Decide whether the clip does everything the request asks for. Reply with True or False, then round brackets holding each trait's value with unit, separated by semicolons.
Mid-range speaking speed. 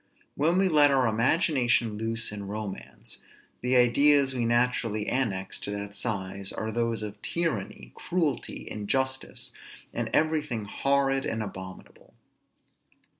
False (125 wpm)